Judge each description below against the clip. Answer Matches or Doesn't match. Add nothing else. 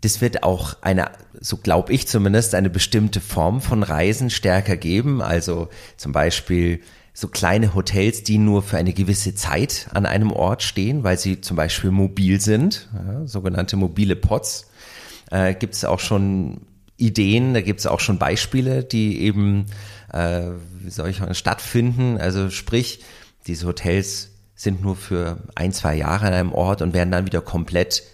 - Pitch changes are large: Doesn't match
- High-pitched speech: Doesn't match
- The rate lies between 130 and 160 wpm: Doesn't match